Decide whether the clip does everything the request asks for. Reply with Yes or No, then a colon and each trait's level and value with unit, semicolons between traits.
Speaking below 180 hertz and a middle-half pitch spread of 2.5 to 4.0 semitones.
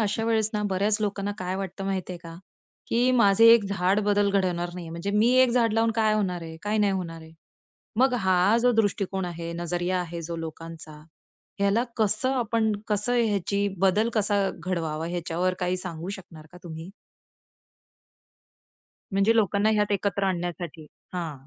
No: high, 195 Hz; average, 3.4 semitones